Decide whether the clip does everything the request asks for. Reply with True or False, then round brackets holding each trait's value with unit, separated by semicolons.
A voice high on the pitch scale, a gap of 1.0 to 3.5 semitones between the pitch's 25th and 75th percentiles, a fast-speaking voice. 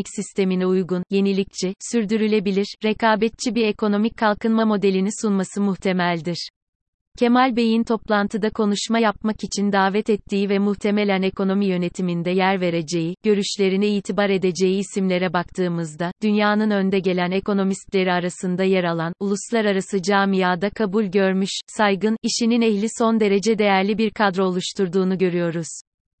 False (200 Hz; 2.4 semitones; 115 wpm)